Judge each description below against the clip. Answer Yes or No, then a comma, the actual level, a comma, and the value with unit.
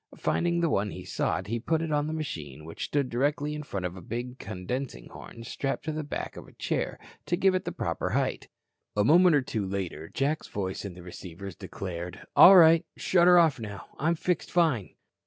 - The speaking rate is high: Yes, fast, 210 wpm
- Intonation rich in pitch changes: Yes, wide, 8.5 semitones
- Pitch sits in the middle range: No, low, 130 Hz